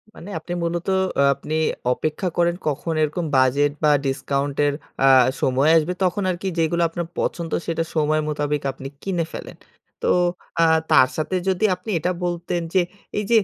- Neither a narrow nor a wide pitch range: Yes, average, 3.1 semitones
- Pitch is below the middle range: No, medium, 160 Hz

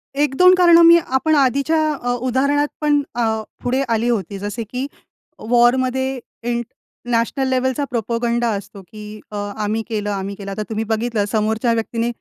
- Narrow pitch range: No, average, 3.3 semitones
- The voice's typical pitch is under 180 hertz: No, high, 240 Hz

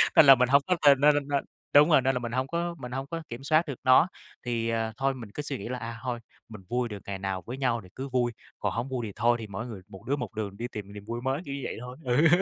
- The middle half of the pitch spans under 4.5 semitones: Yes, average, 3.1 semitones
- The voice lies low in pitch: Yes, low, 125 Hz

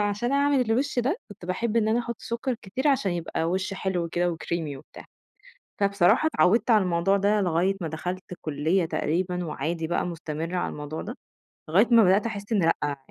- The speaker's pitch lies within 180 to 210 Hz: Yes, high, 190 Hz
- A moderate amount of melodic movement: Yes, average, 4.9 semitones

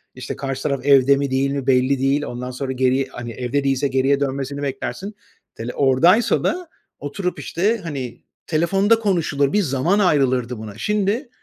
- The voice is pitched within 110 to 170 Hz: Yes, medium, 140 Hz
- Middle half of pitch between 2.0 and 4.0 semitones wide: No, average, 4.7 semitones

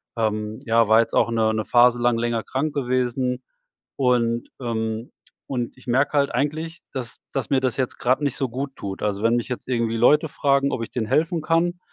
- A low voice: Yes, low, 125 Hz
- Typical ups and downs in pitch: Yes, average, 3.1 semitones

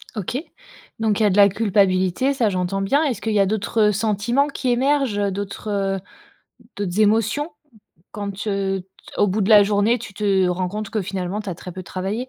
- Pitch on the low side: No, high, 205 Hz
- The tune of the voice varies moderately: No, narrow, 2.3 semitones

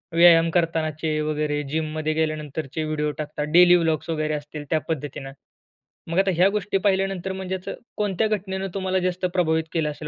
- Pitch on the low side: No, medium, 165 Hz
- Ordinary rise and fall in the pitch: Yes, average, 3.4 semitones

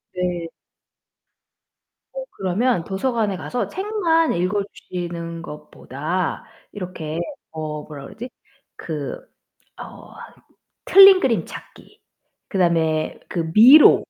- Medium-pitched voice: Yes, medium, 180 Hz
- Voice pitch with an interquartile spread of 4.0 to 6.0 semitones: No, wide, 6.8 semitones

